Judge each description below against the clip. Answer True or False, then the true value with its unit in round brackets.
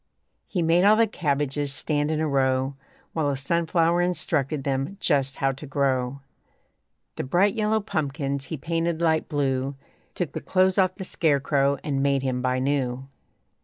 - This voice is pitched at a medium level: True (145 Hz)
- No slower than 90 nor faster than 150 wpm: False (165 wpm)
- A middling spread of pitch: True (3.7 semitones)